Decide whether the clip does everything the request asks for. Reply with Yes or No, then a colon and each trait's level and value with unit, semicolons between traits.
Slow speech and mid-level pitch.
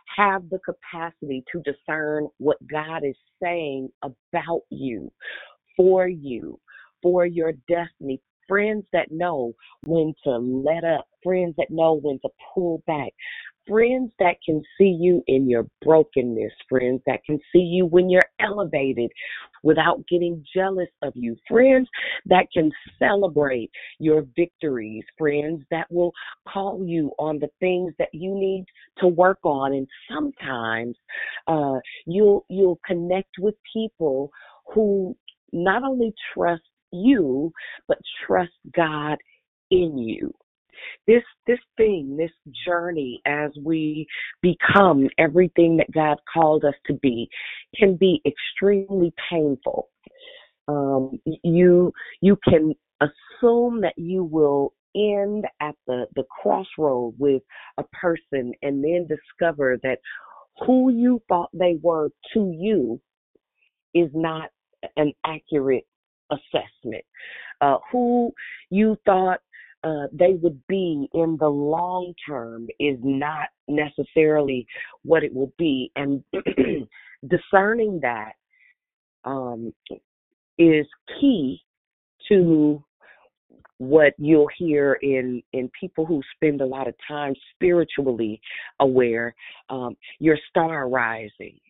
Yes: slow, 120 wpm; medium, 160 Hz